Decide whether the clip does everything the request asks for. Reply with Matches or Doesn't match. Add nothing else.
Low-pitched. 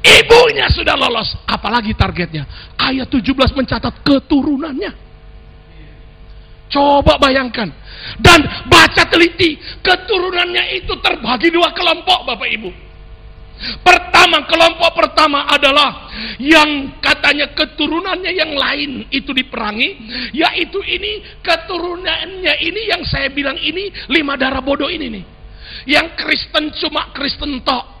Doesn't match